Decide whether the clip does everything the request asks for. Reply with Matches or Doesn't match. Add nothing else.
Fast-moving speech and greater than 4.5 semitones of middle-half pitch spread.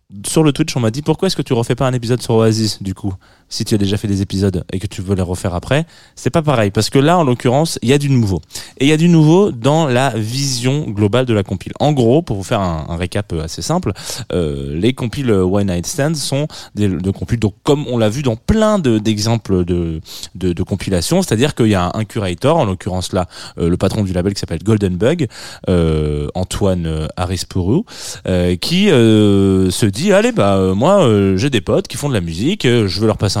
Matches